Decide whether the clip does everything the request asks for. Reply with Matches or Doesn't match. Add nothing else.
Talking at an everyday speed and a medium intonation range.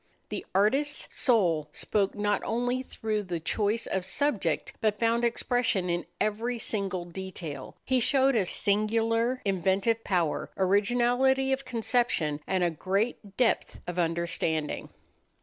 Doesn't match